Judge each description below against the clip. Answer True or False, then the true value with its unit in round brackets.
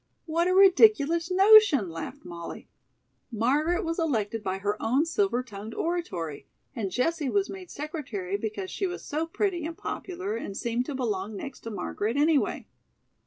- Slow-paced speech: False (160 wpm)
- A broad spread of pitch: True (8.5 semitones)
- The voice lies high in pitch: True (280 Hz)